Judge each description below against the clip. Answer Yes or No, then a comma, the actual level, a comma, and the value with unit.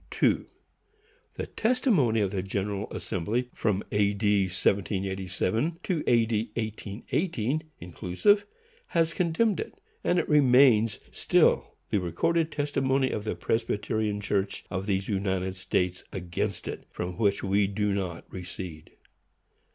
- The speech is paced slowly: Yes, slow, 130 wpm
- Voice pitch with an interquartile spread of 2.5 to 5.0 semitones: No, wide, 5.5 semitones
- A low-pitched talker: Yes, low, 105 Hz